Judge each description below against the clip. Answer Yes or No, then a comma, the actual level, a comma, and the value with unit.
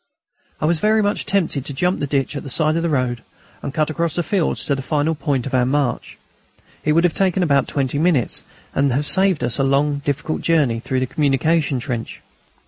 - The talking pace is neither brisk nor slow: No, fast, 220 wpm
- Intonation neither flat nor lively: Yes, average, 3.5 semitones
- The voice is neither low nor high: Yes, medium, 145 Hz